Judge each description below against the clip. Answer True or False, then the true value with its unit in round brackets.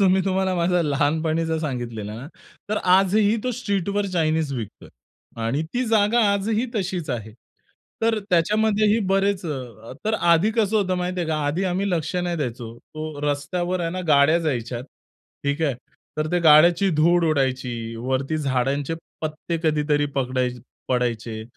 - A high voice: False (160 Hz)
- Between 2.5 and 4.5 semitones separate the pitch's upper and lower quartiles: False (5.4 semitones)